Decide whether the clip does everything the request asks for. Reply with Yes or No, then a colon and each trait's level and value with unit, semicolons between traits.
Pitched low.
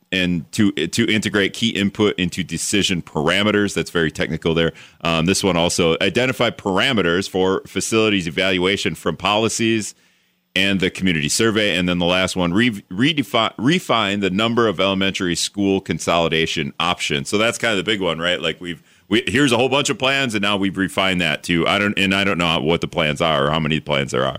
Yes: very low, 95 Hz